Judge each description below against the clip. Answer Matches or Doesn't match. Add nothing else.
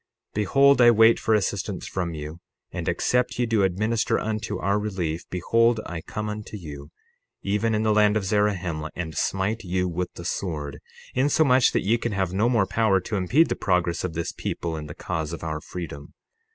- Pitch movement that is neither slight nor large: Matches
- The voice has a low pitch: Matches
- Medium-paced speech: Matches